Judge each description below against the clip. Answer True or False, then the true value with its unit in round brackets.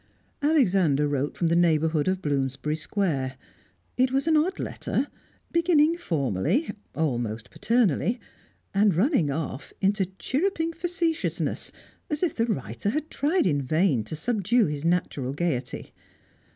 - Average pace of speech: False (130 wpm)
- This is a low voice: False (185 Hz)